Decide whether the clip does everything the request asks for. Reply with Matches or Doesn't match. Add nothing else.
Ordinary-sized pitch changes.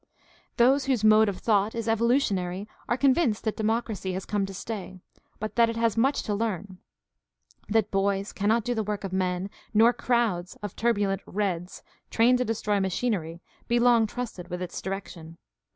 Matches